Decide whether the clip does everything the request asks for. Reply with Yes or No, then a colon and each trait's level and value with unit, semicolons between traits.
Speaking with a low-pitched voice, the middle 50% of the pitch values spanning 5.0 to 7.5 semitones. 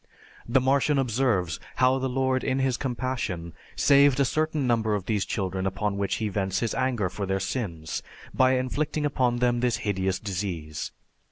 Yes: low, 120 Hz; average, 5.3 semitones